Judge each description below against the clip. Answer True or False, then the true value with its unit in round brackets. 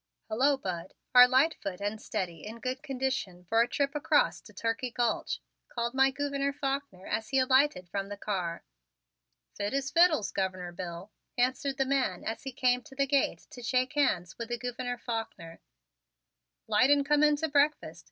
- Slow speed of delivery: False (175 wpm)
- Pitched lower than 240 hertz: False (250 Hz)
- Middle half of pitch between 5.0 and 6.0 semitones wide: True (5.4 semitones)